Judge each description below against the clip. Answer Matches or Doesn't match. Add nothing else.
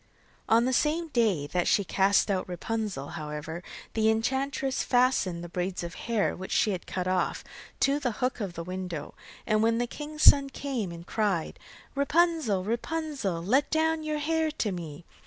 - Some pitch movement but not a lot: Doesn't match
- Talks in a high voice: Matches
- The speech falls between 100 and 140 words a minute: Doesn't match